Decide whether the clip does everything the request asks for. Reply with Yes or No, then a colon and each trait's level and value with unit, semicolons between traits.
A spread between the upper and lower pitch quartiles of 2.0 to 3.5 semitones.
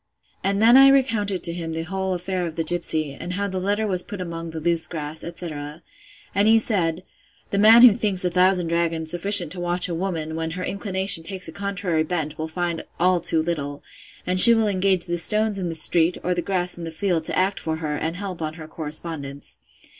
Yes: average, 3.1 semitones